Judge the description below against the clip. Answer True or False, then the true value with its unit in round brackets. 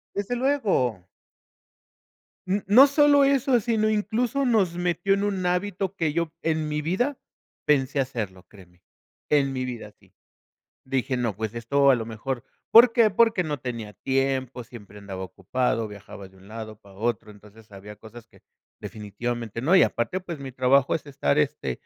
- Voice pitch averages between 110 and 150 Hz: True (135 Hz)